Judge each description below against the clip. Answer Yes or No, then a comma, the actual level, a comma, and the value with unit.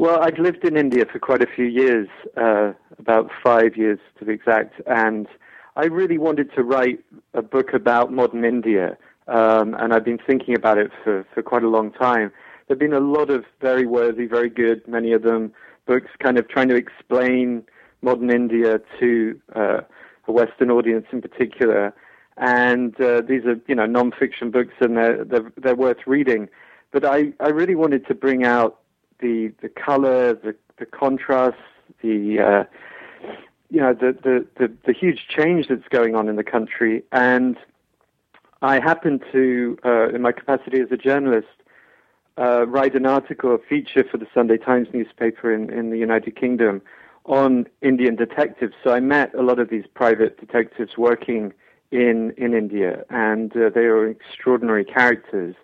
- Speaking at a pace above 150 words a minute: Yes, average, 175 wpm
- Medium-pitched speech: No, low, 120 Hz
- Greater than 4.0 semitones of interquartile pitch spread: No, narrow, 2.5 semitones